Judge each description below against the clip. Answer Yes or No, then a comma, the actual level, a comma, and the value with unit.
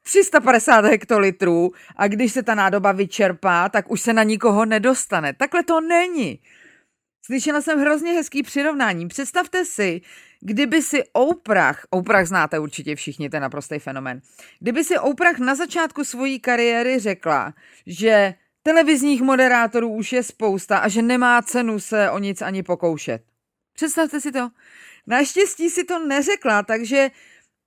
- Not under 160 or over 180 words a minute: No, average, 140 wpm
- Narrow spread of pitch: No, wide, 6.6 semitones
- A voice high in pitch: Yes, high, 235 Hz